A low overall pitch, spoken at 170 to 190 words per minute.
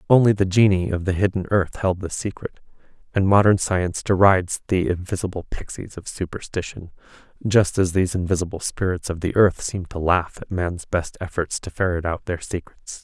Yes: very low, 90 Hz; average, 180 wpm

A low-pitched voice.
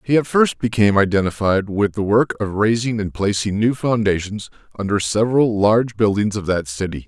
Yes: low, 105 Hz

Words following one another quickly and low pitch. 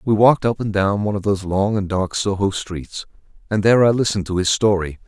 Yes: fast, 235 wpm; low, 100 Hz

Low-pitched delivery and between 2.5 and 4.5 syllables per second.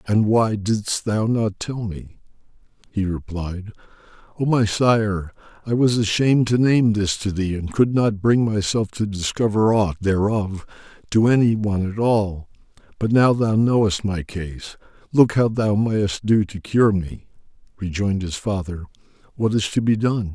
Yes: low, 105 Hz; 4.4 syllables/s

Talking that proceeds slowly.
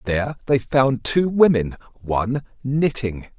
Yes: slow, 125 wpm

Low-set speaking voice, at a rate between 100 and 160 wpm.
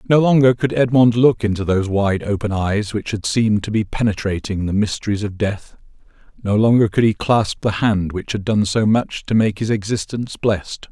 No: low, 105 Hz; fast, 205 wpm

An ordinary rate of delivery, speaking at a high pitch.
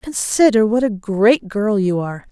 Yes: average, 180 wpm; high, 215 Hz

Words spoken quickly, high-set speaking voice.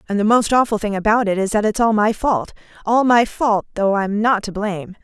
Yes: fast, 240 wpm; high, 210 Hz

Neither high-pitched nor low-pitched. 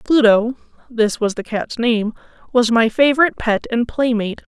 No: high, 235 Hz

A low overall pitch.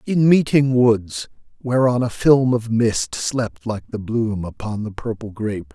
Yes: low, 115 Hz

